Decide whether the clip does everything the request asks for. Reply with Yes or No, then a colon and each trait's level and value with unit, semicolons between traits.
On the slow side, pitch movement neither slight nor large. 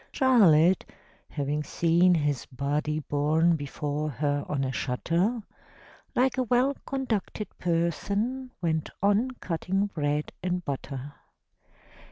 No: slow, 110 wpm; wide, 5.8 semitones